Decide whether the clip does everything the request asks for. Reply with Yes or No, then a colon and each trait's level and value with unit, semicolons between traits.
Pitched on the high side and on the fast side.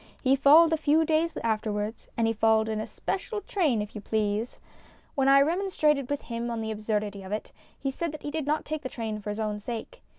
Yes: high, 235 Hz; fast, 230 wpm